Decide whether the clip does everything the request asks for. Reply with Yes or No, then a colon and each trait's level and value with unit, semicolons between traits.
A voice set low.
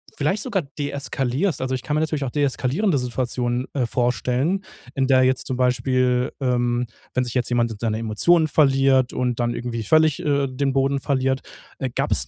Yes: low, 130 Hz